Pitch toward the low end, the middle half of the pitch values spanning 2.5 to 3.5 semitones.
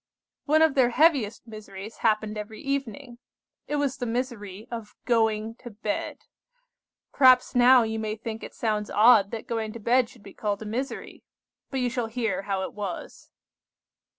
No: high, 225 Hz; average, 2.8 semitones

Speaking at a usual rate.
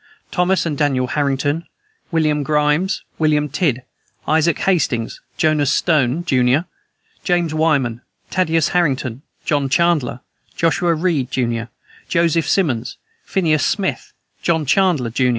No: slow, 115 wpm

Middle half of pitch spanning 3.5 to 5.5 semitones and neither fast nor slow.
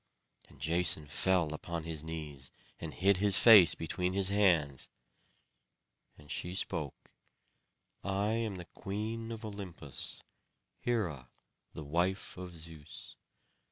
No: average, 4.2 semitones; slow, 120 wpm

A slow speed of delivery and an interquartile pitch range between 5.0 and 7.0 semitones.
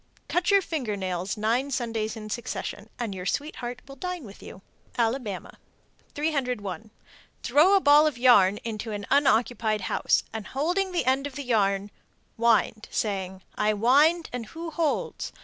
No: average, 155 wpm; wide, 5.4 semitones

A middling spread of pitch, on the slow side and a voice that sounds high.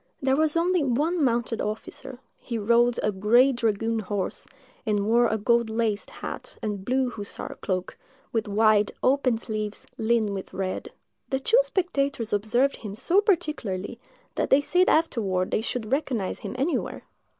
No: average, 4.5 semitones; average, 155 wpm; high, 235 Hz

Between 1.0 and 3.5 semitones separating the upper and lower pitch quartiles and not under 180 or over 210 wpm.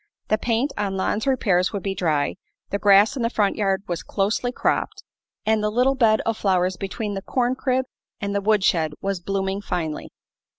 Yes: average, 2.8 semitones; average, 195 wpm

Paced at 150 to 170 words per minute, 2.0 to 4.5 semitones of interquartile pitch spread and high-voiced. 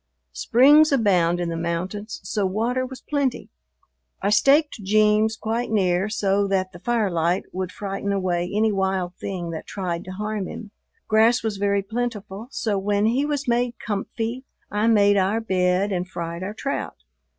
Yes: average, 160 wpm; average, 3.3 semitones; high, 205 Hz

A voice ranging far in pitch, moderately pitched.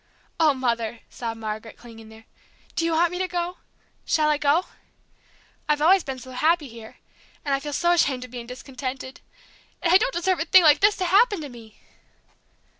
No: wide, 6.1 semitones; very high, 290 Hz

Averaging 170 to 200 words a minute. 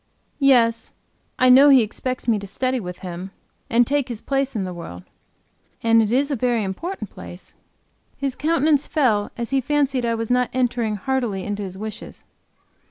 Yes: average, 175 wpm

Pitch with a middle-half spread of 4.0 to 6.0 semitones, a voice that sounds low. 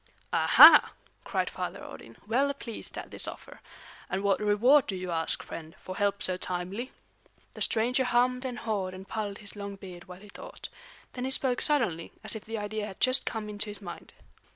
No: average, 4.3 semitones; high, 210 Hz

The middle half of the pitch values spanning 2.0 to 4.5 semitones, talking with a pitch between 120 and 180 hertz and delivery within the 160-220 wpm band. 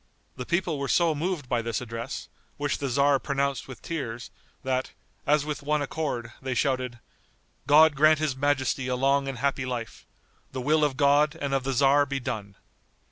Yes: narrow, 2.4 semitones; medium, 140 Hz; average, 185 wpm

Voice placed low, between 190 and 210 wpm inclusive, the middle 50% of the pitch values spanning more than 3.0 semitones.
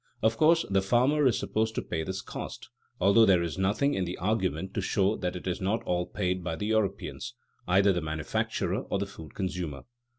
Yes: very low, 95 Hz; fast, 205 wpm; average, 3.5 semitones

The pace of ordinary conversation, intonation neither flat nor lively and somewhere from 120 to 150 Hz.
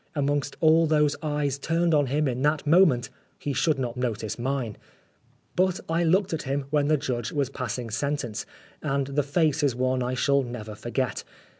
Yes: average, 180 wpm; average, 3.3 semitones; medium, 140 Hz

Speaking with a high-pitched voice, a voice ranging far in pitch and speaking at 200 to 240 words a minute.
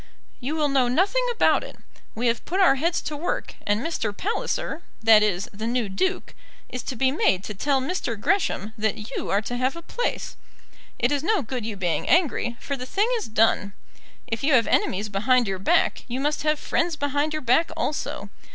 Yes: very high, 260 Hz; wide, 6.0 semitones; fast, 205 wpm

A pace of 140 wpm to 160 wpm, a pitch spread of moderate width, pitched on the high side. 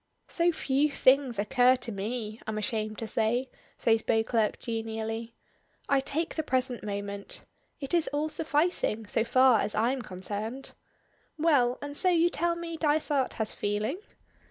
Yes: average, 150 wpm; average, 4.9 semitones; high, 245 Hz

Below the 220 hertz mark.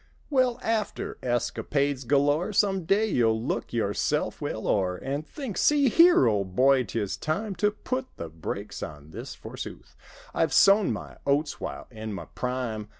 Yes: medium, 140 Hz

